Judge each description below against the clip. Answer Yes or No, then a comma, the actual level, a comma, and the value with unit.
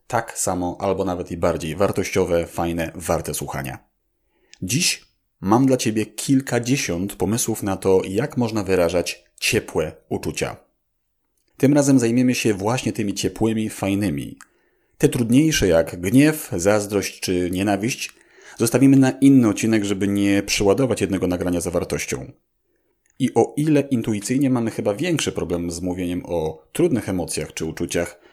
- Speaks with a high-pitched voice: No, low, 100 Hz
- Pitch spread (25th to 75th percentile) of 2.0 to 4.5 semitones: No, average, 5.3 semitones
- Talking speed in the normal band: Yes, average, 135 wpm